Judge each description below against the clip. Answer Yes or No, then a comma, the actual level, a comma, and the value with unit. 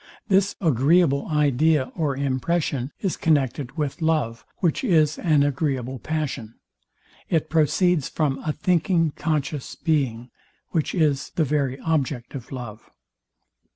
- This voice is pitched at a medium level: Yes, medium, 150 Hz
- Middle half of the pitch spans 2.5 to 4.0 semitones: Yes, average, 3.4 semitones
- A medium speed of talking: No, slow, 120 wpm